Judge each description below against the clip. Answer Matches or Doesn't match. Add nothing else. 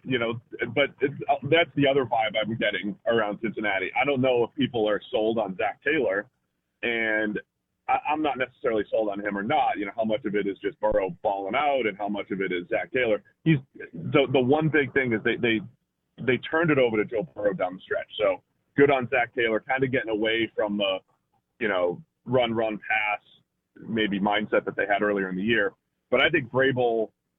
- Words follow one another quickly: Matches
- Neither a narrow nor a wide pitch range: Matches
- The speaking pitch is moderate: Doesn't match